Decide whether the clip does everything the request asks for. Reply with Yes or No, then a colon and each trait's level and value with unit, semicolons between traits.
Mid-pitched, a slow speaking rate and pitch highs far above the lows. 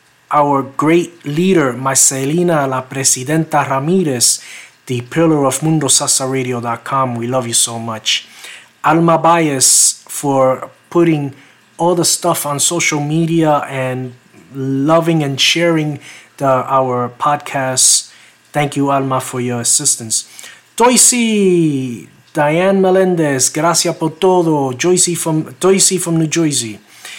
No: medium, 145 Hz; slow, 110 wpm; average, 4.1 semitones